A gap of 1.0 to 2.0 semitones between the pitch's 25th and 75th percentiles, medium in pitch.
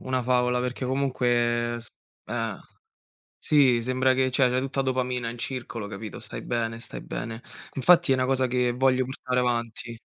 No: narrow, 1.6 semitones; low, 125 Hz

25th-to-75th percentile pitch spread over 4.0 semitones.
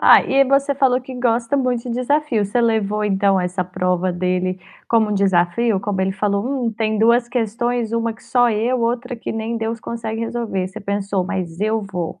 No: average, 3.6 semitones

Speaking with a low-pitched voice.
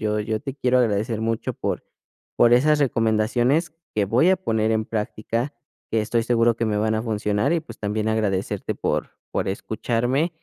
Yes: low, 115 Hz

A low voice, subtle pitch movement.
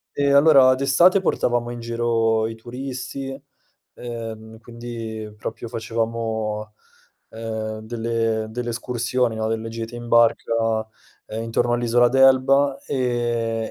Yes: low, 115 Hz; narrow, 1.7 semitones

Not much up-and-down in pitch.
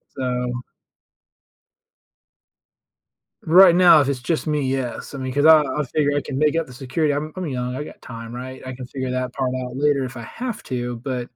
No: average, 3.0 semitones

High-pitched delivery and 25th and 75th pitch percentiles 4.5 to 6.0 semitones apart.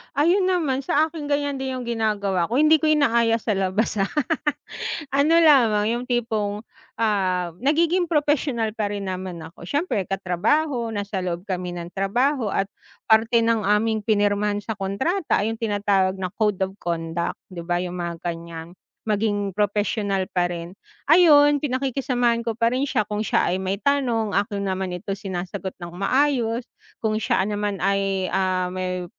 Yes: high, 210 Hz; average, 5.0 semitones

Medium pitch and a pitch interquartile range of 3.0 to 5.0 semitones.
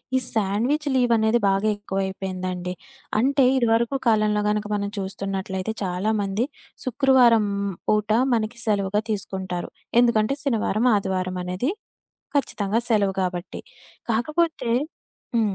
No: high, 210 Hz; average, 3.4 semitones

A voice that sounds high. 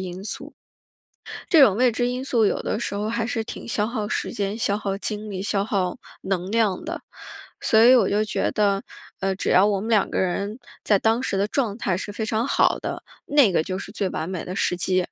Yes: high, 205 Hz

